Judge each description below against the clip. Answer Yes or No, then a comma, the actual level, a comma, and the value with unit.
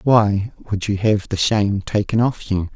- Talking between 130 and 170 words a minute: No, average, 195 wpm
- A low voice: Yes, low, 105 Hz